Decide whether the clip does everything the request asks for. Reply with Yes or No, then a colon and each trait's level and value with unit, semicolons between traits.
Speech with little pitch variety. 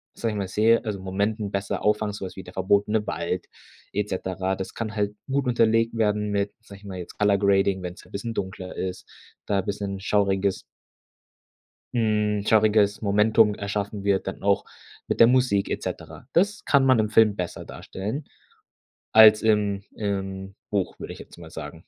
Yes: narrow, 1.9 semitones